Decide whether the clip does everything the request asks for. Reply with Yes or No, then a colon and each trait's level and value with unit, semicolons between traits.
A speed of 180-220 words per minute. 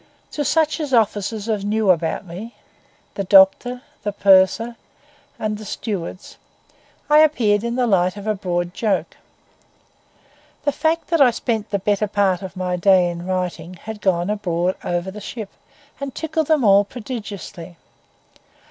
No: average, 150 wpm